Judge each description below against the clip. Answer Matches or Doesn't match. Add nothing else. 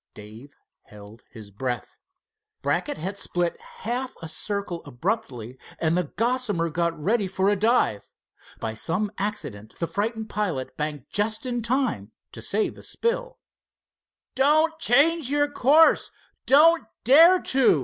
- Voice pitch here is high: Matches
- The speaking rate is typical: Doesn't match